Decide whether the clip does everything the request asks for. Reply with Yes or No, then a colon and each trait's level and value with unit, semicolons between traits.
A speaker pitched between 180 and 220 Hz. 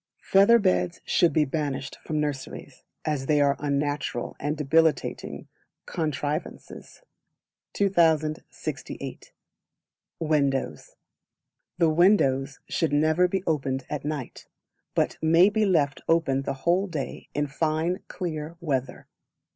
No: medium, 155 Hz